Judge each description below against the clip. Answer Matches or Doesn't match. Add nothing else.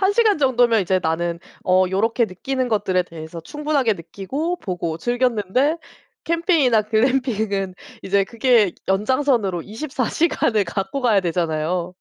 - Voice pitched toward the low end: Doesn't match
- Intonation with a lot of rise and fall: Matches